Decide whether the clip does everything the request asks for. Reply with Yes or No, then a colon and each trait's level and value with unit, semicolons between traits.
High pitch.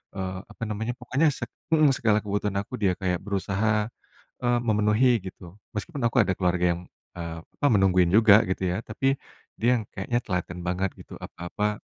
No: low, 100 Hz